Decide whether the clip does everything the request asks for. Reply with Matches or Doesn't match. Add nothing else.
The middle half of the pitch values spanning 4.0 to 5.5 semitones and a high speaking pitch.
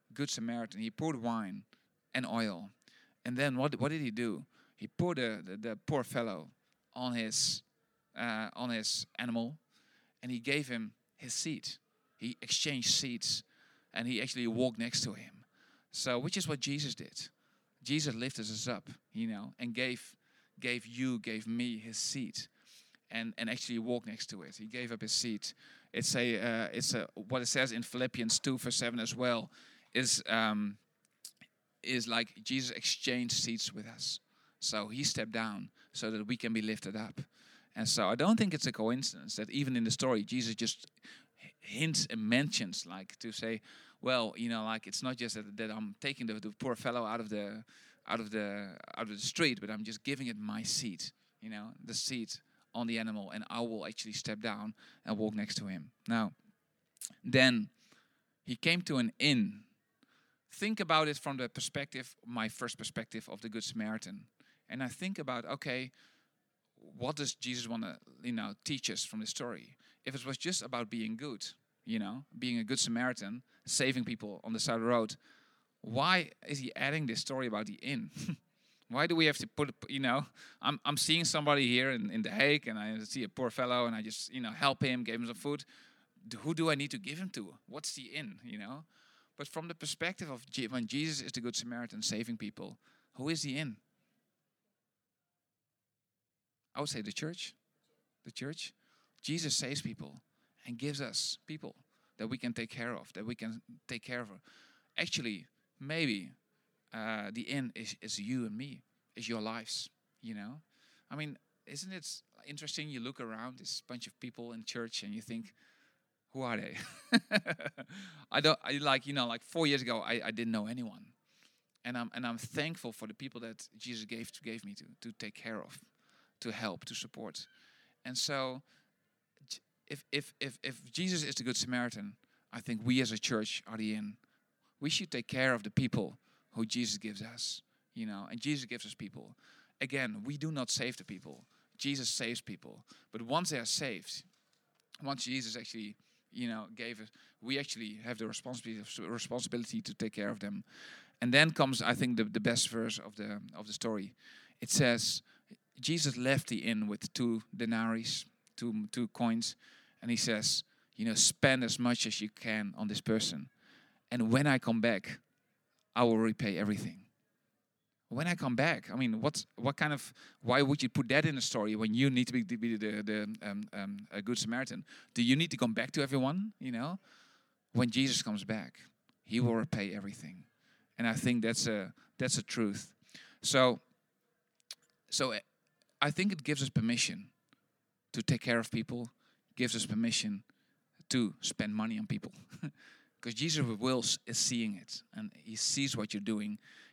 Doesn't match